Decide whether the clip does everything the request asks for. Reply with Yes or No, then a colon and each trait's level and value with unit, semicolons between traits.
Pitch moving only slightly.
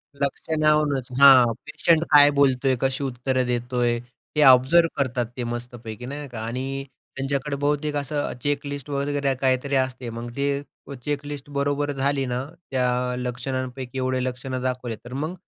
Yes: narrow, 2.2 semitones